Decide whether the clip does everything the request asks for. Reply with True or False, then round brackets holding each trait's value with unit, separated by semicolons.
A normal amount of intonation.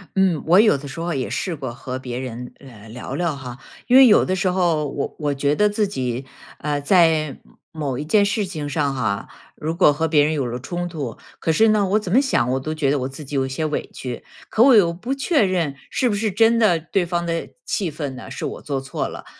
False (5.7 semitones)